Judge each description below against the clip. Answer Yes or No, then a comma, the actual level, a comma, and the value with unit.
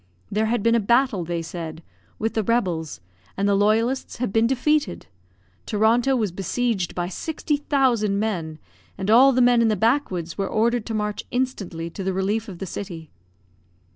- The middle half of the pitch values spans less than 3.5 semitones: No, average, 4.4 semitones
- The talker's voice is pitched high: Yes, high, 215 Hz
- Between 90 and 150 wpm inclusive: No, average, 175 wpm